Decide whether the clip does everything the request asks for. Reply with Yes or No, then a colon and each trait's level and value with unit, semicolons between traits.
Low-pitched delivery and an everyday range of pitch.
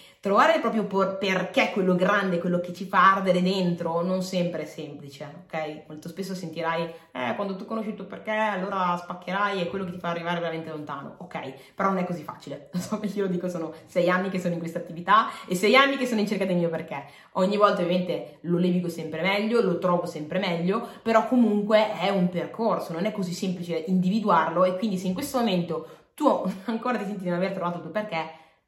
No: medium, 185 Hz; average, 3.0 semitones